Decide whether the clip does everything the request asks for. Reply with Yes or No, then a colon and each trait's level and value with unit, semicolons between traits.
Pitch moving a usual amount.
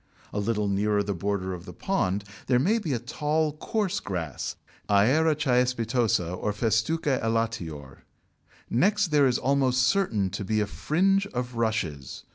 No: wide, 6.5 semitones